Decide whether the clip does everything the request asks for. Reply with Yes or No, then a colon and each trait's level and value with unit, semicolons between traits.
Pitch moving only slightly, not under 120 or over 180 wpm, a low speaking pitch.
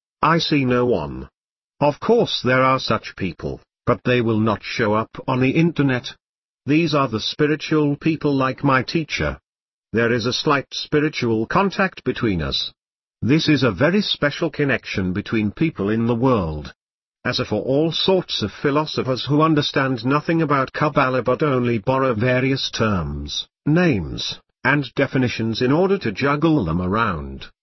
No: average, 5.0 semitones; average, 155 wpm; low, 130 Hz